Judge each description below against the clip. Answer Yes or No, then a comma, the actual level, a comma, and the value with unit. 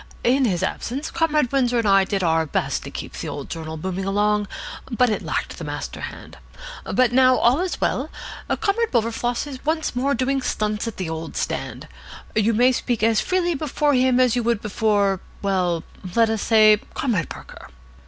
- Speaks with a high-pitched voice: Yes, high, 230 Hz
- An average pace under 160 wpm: No, average, 185 wpm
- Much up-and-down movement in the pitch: No, average, 4.3 semitones